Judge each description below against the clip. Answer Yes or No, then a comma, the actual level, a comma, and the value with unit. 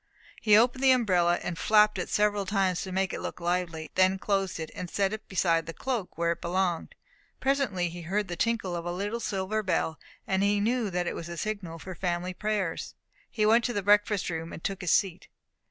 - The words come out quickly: Yes, fast, 215 wpm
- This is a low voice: No, high, 190 Hz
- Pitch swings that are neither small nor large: Yes, average, 3.3 semitones